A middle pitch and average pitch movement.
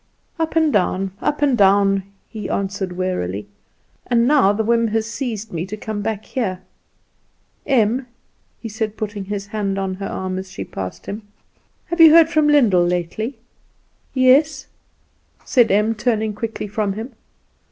No: high, 215 Hz; average, 3.9 semitones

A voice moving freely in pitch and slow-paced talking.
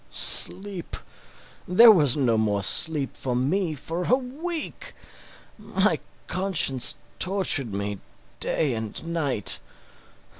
Yes: wide, 7.8 semitones; slow, 105 wpm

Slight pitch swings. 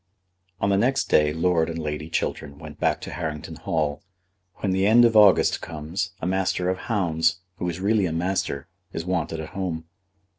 No: average, 3.2 semitones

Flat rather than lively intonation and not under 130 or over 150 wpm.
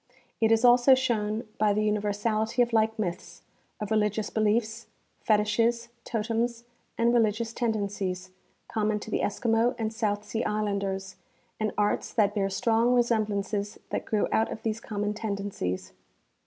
Yes: narrow, 1.8 semitones; average, 145 wpm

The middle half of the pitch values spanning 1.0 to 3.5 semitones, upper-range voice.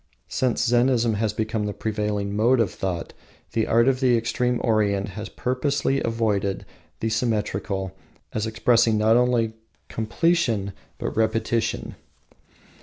No: narrow, 2.5 semitones; low, 110 Hz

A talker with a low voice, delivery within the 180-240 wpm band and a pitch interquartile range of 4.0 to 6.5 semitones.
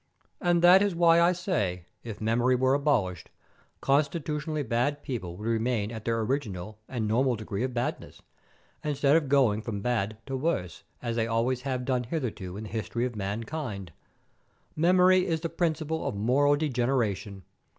No: low, 125 Hz; average, 160 wpm; wide, 5.6 semitones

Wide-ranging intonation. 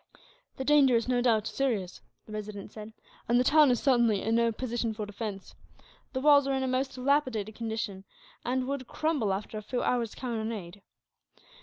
No: average, 3.4 semitones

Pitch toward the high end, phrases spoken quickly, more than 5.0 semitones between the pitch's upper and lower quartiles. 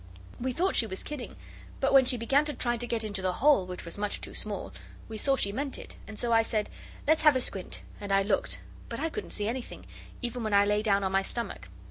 No: high, 230 Hz; fast, 245 wpm; average, 4.7 semitones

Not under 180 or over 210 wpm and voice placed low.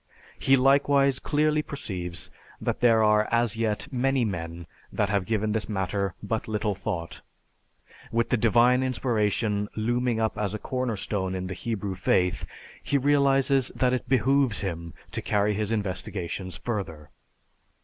No: average, 150 wpm; low, 110 Hz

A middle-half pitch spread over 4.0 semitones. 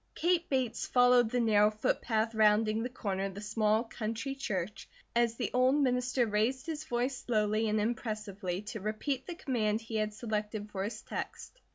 No: average, 2.9 semitones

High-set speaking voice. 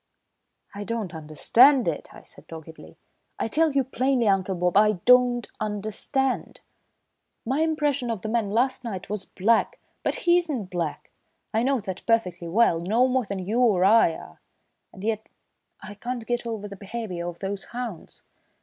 Yes: high, 220 Hz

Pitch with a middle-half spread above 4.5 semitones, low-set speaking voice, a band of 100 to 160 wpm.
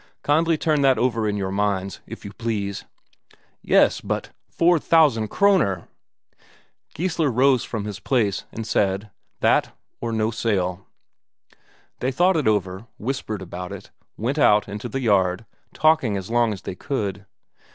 Yes: wide, 5.4 semitones; low, 110 Hz; average, 150 wpm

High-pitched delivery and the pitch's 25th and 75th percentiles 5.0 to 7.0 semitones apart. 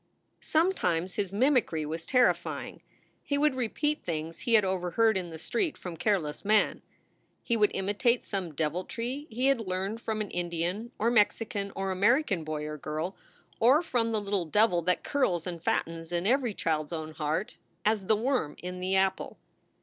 Yes: high, 195 Hz; average, 5.3 semitones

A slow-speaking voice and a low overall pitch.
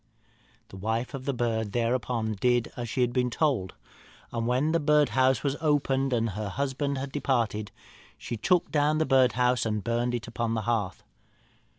No: average, 170 wpm; low, 125 Hz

